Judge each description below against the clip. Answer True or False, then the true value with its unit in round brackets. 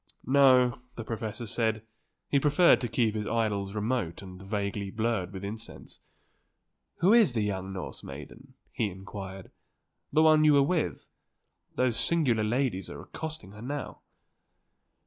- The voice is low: True (115 Hz)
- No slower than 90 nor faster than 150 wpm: True (145 wpm)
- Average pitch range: True (5.0 semitones)